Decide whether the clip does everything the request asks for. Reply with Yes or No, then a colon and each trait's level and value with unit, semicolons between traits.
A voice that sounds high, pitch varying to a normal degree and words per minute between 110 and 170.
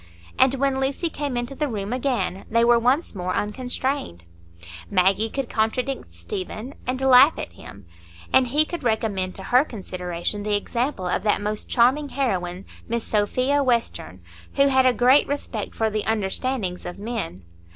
Yes: high, 235 Hz; average, 5.0 semitones; average, 160 wpm